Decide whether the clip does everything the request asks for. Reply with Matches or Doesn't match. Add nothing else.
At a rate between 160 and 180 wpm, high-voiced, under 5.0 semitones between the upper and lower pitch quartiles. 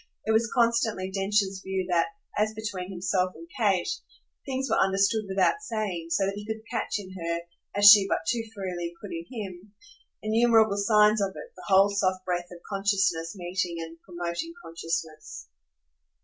Matches